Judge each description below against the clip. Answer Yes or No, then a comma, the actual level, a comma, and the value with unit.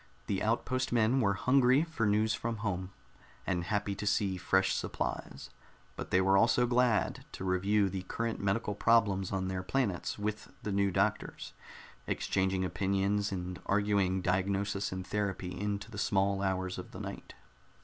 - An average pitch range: No, narrow, 2.3 semitones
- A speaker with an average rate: Yes, average, 160 wpm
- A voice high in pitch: No, low, 100 Hz